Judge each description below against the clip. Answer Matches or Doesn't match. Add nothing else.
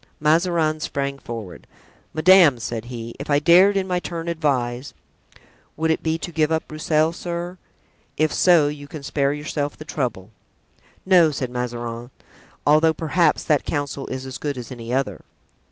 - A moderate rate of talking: Matches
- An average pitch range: Matches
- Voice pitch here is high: Doesn't match